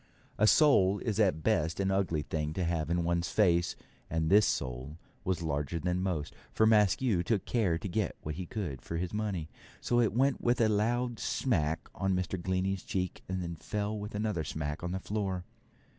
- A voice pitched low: Yes, very low, 95 Hz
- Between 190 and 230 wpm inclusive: Yes, average, 200 wpm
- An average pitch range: Yes, average, 4.1 semitones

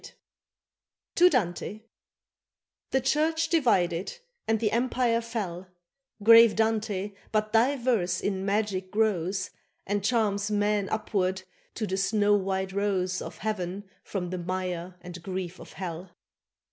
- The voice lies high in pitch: Yes, high, 205 Hz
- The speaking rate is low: Yes, slow, 130 wpm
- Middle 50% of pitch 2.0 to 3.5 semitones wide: Yes, average, 3.1 semitones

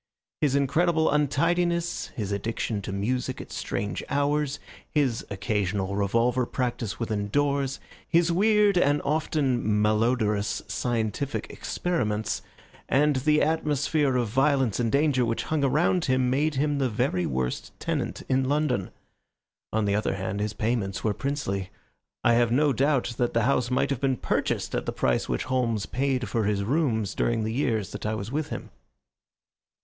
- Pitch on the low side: Yes, low, 125 Hz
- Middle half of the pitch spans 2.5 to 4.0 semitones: No, average, 5.1 semitones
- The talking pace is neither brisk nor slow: Yes, average, 155 wpm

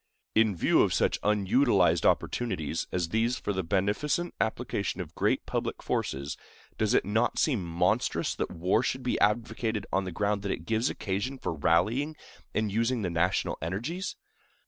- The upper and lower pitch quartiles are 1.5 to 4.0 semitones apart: No, average, 4.6 semitones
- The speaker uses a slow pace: No, average, 165 wpm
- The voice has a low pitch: Yes, low, 105 Hz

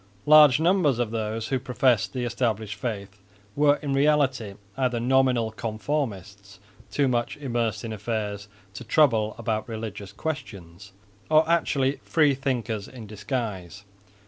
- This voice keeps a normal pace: No, slow, 130 wpm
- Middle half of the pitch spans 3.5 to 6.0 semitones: Yes, average, 4.2 semitones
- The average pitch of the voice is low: Yes, low, 120 Hz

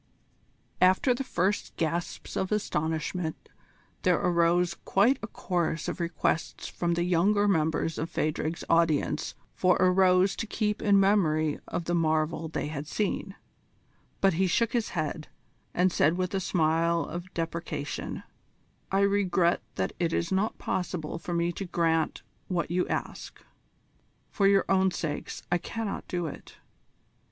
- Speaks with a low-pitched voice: No, medium, 175 Hz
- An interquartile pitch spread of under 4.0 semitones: Yes, average, 2.8 semitones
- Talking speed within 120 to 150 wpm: Yes, average, 145 wpm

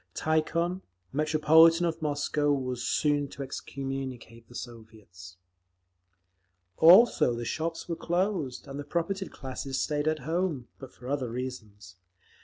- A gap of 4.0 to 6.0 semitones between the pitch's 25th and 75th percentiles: Yes, average, 4.4 semitones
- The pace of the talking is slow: Yes, slow, 120 wpm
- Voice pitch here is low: No, medium, 145 Hz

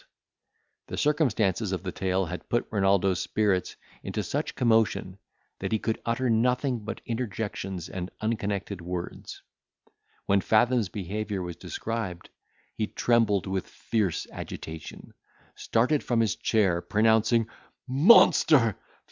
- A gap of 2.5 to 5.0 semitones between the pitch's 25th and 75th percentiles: Yes, average, 3.5 semitones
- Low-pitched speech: Yes, low, 110 Hz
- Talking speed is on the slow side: Yes, slow, 120 wpm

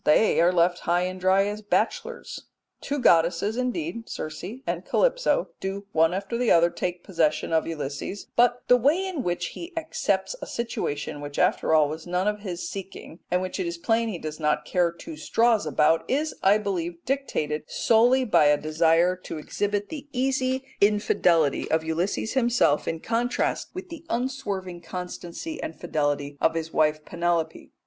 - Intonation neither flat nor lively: No, wide, 6.5 semitones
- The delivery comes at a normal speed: Yes, average, 170 wpm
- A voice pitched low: No, medium, 185 Hz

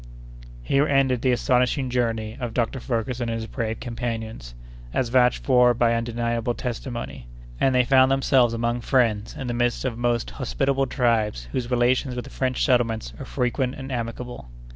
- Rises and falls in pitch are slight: Yes, narrow, 1.8 semitones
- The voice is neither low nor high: No, low, 120 Hz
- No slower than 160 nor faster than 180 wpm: Yes, average, 165 wpm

